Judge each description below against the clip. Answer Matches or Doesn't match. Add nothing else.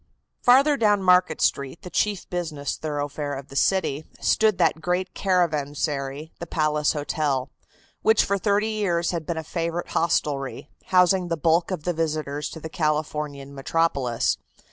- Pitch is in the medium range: Matches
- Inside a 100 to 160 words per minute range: Matches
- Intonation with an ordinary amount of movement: Matches